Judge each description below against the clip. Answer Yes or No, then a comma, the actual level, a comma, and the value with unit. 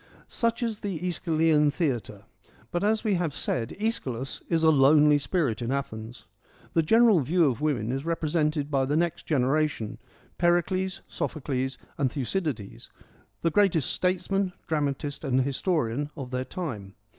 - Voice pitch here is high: No, medium, 150 Hz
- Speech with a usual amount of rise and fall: Yes, average, 4.7 semitones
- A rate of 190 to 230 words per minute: No, average, 145 wpm